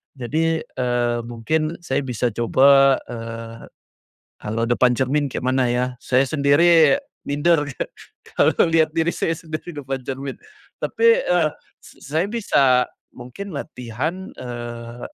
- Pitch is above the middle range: No, low, 135 Hz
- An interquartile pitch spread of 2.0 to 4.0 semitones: No, average, 4.6 semitones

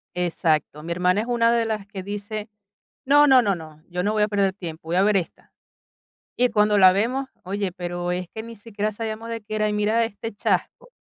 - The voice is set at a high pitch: Yes, high, 205 Hz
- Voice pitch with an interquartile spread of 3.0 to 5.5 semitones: Yes, average, 3.6 semitones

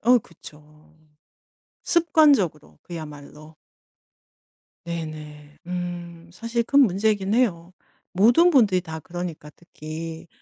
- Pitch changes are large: Yes, wide, 5.8 semitones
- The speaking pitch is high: No, medium, 175 Hz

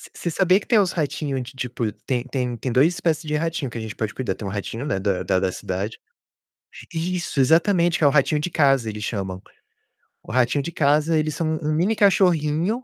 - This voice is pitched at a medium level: Yes, medium, 145 Hz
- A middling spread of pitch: No, wide, 5.8 semitones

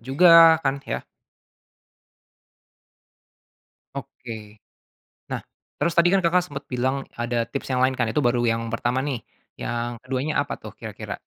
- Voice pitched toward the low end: Yes, low, 130 Hz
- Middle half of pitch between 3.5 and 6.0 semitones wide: Yes, average, 3.9 semitones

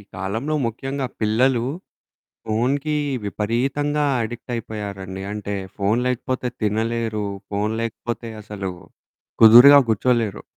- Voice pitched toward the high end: No, low, 115 Hz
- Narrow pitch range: No, average, 3.3 semitones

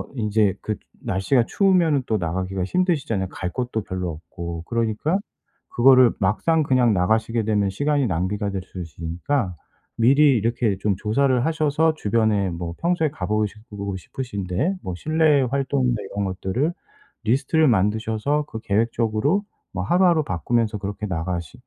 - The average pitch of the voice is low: Yes, low, 110 Hz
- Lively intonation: Yes, wide, 6.4 semitones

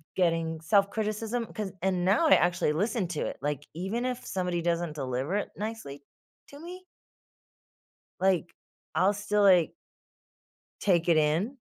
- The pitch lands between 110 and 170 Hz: No, medium, 185 Hz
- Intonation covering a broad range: No, average, 4.4 semitones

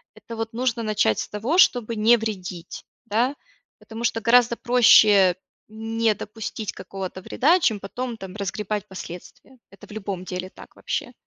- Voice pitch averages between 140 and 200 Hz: No, high, 220 Hz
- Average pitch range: Yes, average, 3.1 semitones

